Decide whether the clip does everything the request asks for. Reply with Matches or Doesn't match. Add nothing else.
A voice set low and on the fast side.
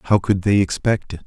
Matches